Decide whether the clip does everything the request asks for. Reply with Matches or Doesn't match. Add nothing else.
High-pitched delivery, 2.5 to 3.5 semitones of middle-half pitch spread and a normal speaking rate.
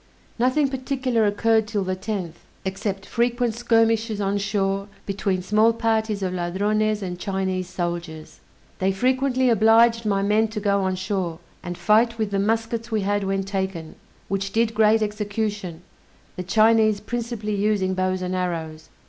Matches